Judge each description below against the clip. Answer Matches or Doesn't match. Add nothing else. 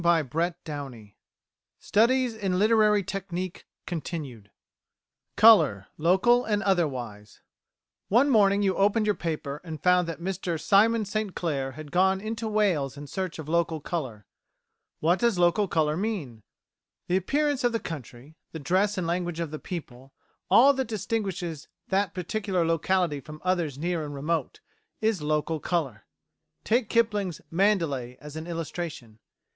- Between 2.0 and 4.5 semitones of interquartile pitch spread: Doesn't match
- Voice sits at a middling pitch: Matches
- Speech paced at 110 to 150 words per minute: Matches